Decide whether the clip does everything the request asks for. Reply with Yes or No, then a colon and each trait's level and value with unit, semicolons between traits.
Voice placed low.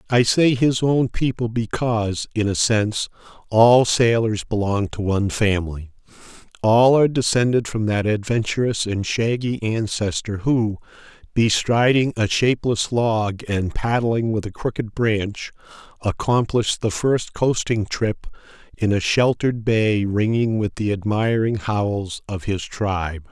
Yes: low, 110 Hz